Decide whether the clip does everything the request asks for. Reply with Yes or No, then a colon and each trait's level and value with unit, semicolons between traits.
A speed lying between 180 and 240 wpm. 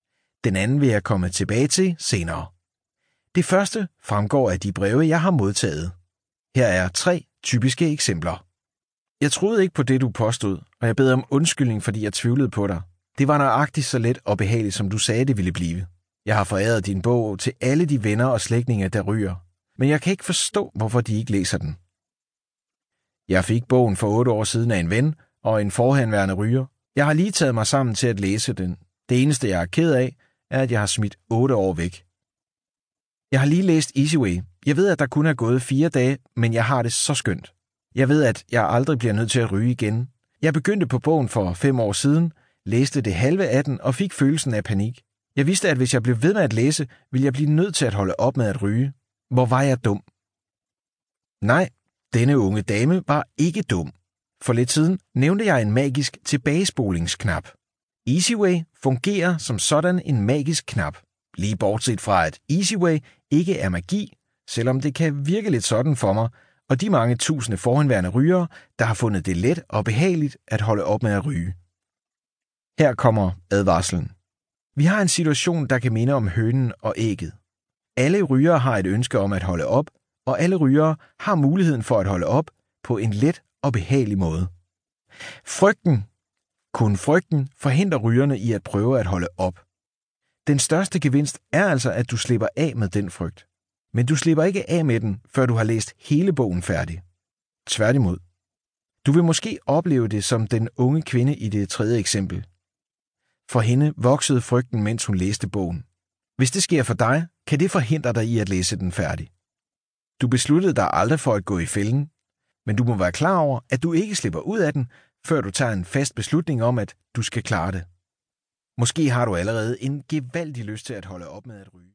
Yes: average, 200 wpm